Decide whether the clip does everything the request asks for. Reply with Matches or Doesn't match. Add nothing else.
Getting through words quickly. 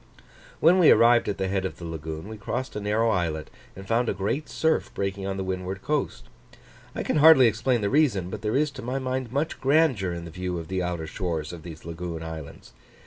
Matches